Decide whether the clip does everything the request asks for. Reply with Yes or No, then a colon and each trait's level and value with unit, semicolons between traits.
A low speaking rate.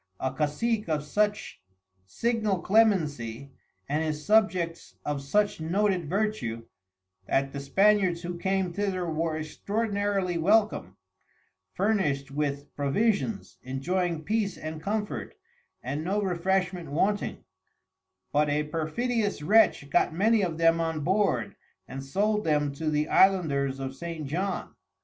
Yes: slow, 125 wpm